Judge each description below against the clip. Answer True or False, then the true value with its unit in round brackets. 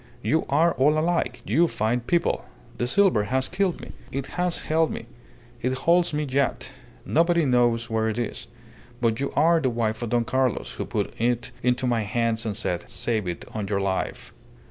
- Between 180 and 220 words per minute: True (190 wpm)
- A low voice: True (125 Hz)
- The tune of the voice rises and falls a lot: True (5.7 semitones)